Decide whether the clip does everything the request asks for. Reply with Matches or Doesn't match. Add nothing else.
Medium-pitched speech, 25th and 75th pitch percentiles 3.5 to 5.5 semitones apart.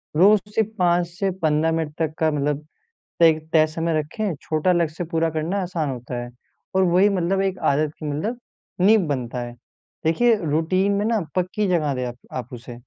Matches